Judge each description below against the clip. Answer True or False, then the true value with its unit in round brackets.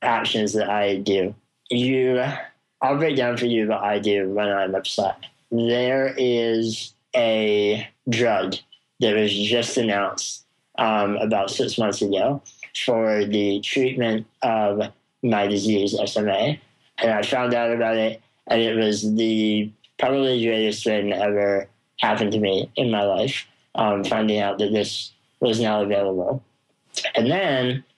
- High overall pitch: False (110 Hz)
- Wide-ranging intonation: False (2.4 semitones)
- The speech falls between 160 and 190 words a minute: False (145 wpm)